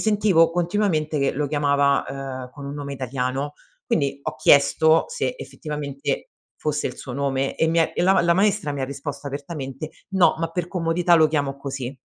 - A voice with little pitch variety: No, average, 3.3 semitones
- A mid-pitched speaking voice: Yes, medium, 145 Hz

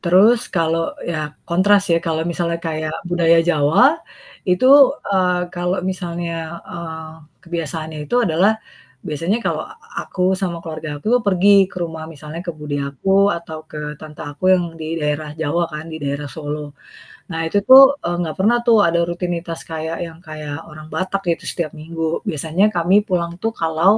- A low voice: No, medium, 165 Hz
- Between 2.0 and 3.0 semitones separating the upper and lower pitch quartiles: Yes, narrow, 2.4 semitones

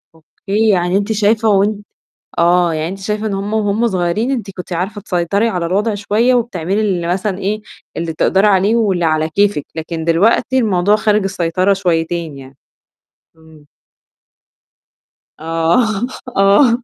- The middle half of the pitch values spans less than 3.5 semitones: No, average, 3.8 semitones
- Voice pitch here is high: Yes, high, 195 Hz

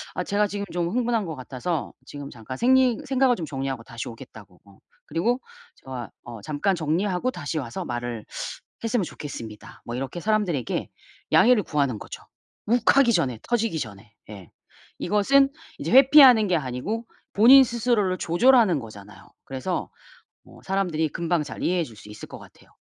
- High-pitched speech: No, medium, 170 Hz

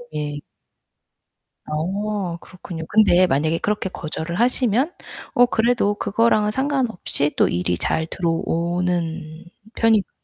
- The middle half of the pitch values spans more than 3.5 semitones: Yes, average, 5.1 semitones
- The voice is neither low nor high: Yes, medium, 180 Hz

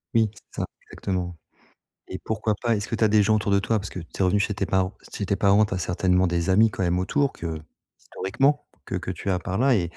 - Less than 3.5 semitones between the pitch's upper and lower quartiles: Yes, average, 2.9 semitones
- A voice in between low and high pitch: No, low, 100 Hz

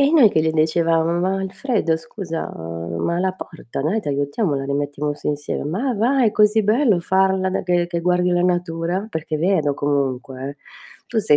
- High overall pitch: No, medium, 170 Hz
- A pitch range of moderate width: Yes, average, 4.7 semitones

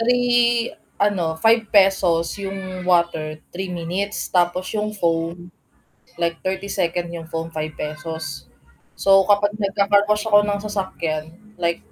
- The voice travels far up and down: No, average, 3.4 semitones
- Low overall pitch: No, medium, 185 Hz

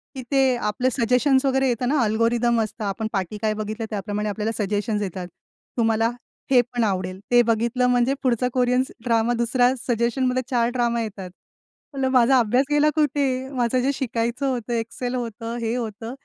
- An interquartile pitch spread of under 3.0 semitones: Yes, narrow, 2.5 semitones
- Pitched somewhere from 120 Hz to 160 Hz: No, high, 235 Hz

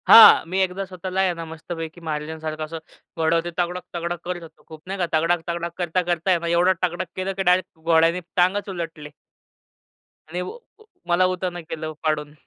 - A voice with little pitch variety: Yes, narrow, 2.0 semitones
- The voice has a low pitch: No, medium, 175 Hz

